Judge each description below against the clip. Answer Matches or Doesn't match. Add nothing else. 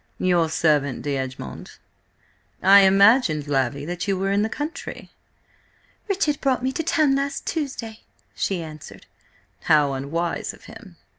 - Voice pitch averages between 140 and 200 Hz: Matches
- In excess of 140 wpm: Doesn't match